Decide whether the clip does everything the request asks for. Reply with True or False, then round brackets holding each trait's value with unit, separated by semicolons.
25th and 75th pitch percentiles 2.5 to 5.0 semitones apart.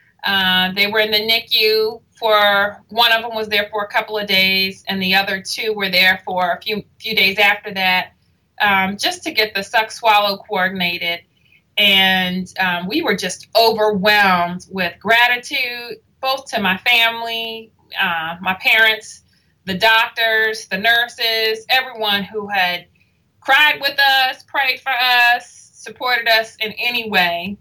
True (3.3 semitones)